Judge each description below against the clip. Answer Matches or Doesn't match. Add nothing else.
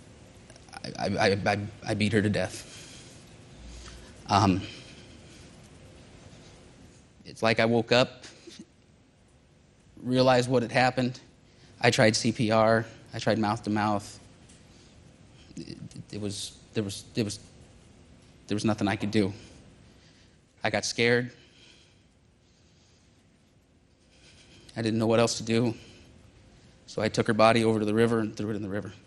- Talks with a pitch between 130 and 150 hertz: Doesn't match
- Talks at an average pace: Doesn't match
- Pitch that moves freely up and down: Doesn't match